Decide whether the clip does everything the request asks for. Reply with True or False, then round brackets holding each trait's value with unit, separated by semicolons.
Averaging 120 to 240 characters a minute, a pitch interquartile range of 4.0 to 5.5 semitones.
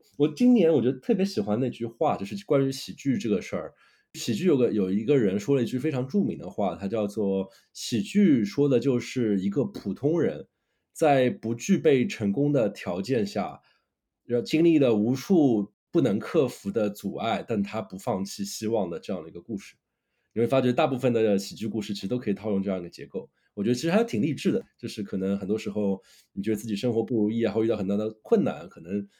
False (325 characters per minute; 5.0 semitones)